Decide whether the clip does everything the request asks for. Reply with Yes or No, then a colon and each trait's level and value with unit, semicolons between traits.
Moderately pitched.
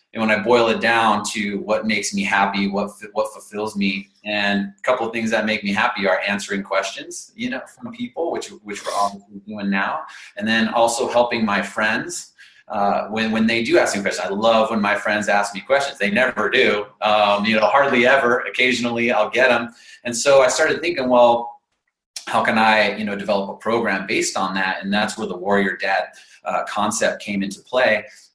No: low, 105 Hz